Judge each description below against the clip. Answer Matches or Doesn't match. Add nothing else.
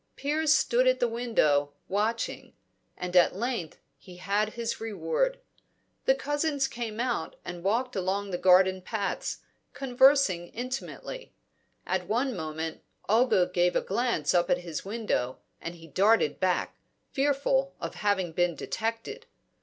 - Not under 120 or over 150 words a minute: Matches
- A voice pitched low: Doesn't match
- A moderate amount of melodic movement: Doesn't match